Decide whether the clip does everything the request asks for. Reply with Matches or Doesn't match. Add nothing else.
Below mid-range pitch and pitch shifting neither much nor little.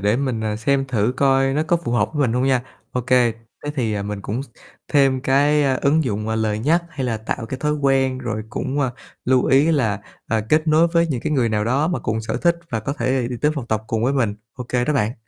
Matches